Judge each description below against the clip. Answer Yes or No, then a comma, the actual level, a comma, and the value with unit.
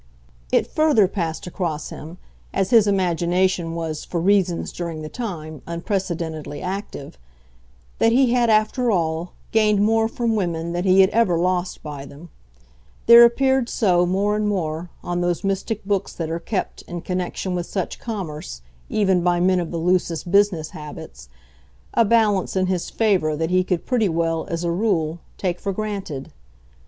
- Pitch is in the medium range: Yes, medium, 180 Hz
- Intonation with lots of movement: No, average, 3.6 semitones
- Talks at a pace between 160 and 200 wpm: Yes, average, 165 wpm